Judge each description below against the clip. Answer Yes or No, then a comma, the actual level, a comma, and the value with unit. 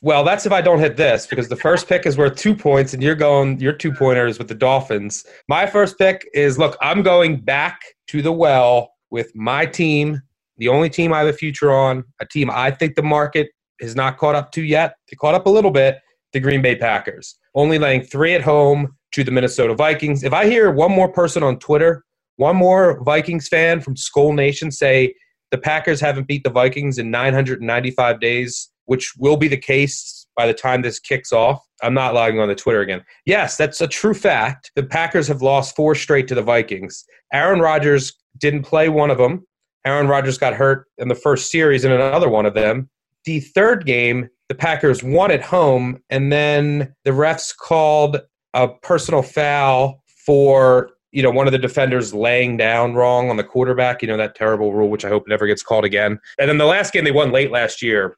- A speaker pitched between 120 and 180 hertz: Yes, medium, 140 Hz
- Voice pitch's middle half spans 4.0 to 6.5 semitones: No, average, 3.5 semitones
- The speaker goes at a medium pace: No, fast, 210 wpm